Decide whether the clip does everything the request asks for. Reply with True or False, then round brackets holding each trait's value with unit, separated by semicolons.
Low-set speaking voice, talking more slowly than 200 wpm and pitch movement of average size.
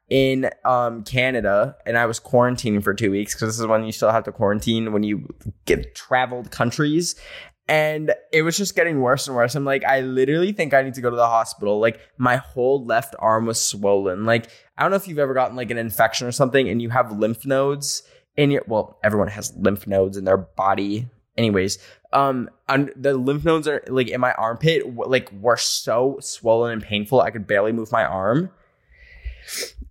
False (120 Hz; 205 wpm; 3.7 semitones)